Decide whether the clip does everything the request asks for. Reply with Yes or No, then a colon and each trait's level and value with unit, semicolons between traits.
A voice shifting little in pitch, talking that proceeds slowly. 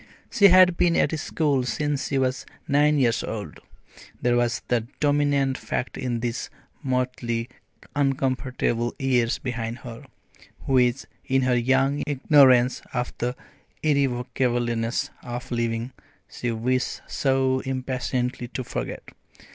Yes: narrow, 2.1 semitones; slow, 120 wpm